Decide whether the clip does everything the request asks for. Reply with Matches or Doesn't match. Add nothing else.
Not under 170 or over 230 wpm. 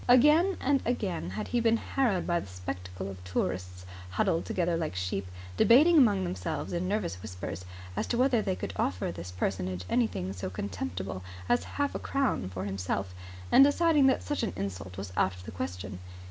Matches